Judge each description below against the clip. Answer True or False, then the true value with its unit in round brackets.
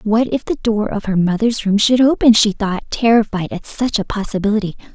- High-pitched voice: True (215 Hz)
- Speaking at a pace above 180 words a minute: True (205 wpm)